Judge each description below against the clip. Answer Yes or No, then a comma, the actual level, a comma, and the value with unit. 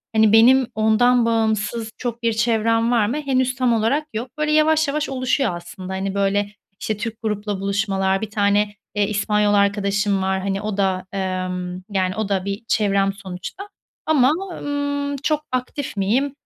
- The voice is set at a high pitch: Yes, high, 215 Hz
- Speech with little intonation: No, average, 4.2 semitones